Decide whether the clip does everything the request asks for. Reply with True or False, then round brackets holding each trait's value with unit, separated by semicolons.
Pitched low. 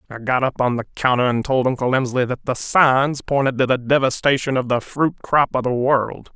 True (130 Hz)